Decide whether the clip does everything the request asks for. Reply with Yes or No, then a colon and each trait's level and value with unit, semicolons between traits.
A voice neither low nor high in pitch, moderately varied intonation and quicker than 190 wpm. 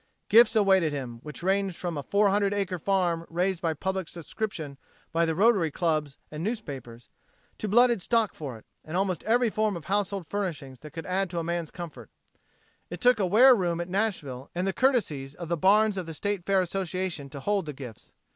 Yes: medium, 180 Hz; average, 4.3 semitones; average, 200 wpm